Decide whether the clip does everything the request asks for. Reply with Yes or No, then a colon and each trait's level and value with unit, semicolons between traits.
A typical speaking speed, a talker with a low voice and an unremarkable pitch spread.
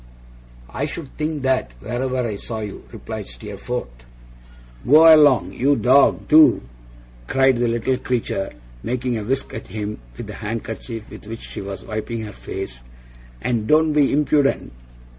Yes: average, 150 wpm; low, 120 Hz; average, 4.3 semitones